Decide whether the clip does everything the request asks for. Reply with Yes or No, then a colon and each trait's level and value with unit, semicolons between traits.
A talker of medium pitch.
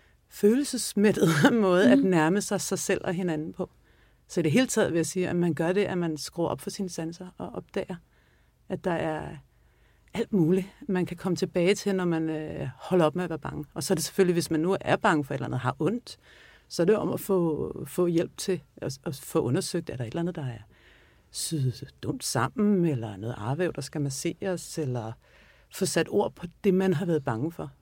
Yes: medium, 170 Hz